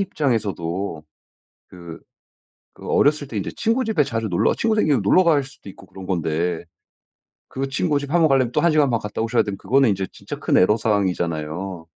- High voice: No, low, 110 Hz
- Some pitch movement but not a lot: No, wide, 7.4 semitones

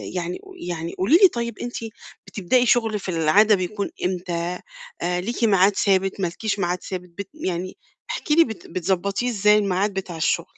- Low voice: No, high, 195 Hz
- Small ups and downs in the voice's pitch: No, average, 3.3 semitones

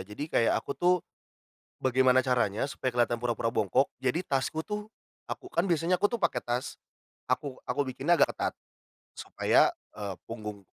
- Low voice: Yes, low, 130 Hz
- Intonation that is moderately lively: No, wide, 6.0 semitones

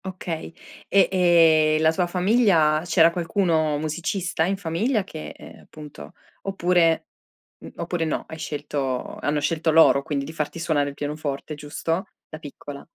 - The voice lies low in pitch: No, medium, 160 Hz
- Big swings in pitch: No, average, 2.7 semitones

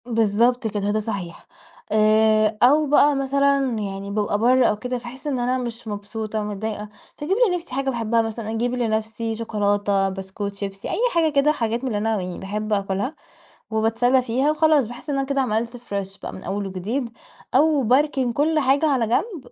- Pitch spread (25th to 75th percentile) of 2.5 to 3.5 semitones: No, average, 4.2 semitones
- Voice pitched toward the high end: Yes, high, 225 Hz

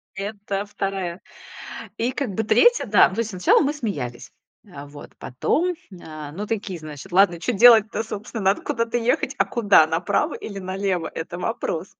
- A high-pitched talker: Yes, high, 200 Hz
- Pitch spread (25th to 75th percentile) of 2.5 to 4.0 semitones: No, average, 4.6 semitones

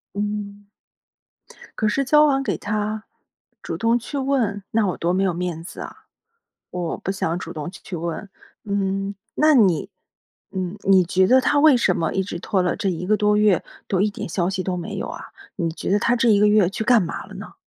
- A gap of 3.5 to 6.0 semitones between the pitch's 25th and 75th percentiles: No, average, 3.1 semitones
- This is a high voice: Yes, high, 200 Hz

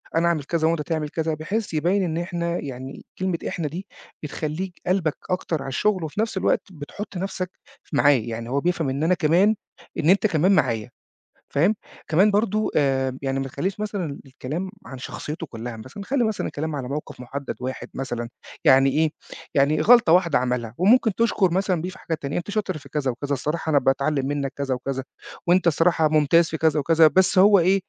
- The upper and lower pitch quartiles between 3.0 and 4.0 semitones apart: No, average, 4.9 semitones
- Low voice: No, medium, 160 Hz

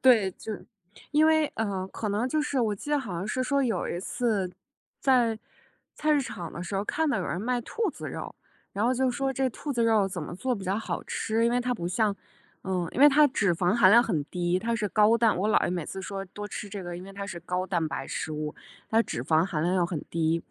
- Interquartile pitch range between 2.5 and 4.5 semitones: No, average, 5.2 semitones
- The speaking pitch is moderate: No, high, 205 Hz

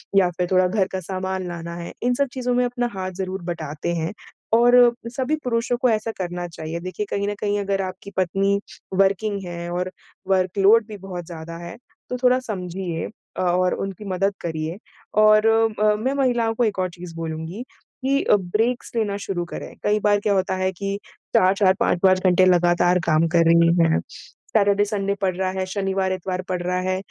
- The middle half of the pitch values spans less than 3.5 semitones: Yes, average, 2.9 semitones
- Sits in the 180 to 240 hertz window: Yes, high, 190 Hz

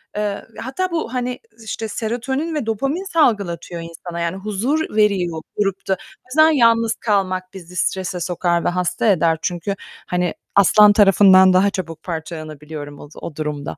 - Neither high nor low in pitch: No, high, 195 Hz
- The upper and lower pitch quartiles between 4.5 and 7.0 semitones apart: Yes, average, 4.8 semitones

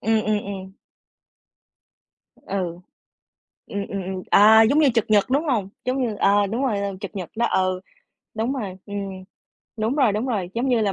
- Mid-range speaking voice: No, high, 210 Hz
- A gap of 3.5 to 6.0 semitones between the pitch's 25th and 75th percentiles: No, average, 3.1 semitones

